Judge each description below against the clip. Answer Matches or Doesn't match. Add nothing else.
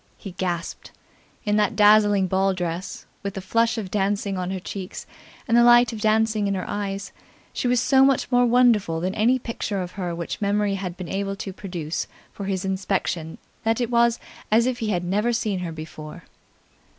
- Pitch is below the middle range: Doesn't match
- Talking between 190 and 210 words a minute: Matches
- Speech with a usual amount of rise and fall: Matches